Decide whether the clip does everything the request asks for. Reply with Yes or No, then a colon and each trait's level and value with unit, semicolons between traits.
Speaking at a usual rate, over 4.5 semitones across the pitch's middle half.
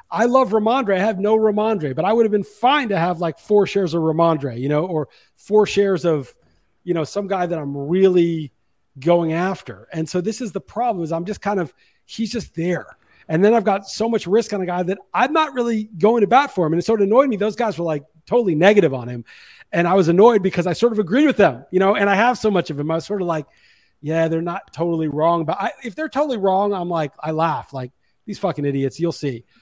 No: fast, 260 wpm; average, 4.9 semitones